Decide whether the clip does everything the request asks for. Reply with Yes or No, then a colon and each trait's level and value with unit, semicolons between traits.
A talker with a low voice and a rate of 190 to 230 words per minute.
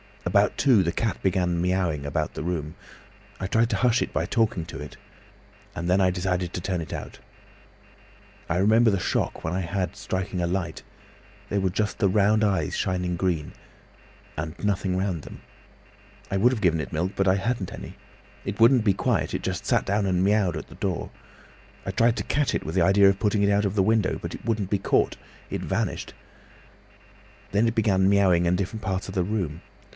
Yes: very low, 95 Hz; average, 200 wpm